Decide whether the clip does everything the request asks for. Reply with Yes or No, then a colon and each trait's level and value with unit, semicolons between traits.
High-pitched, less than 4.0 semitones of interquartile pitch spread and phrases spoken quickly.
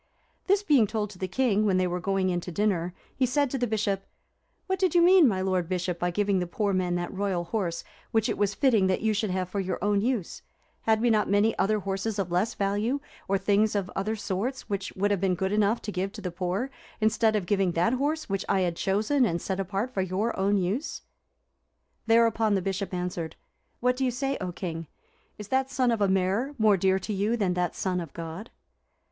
Yes: high, 200 Hz; average, 3.3 semitones; fast, 230 wpm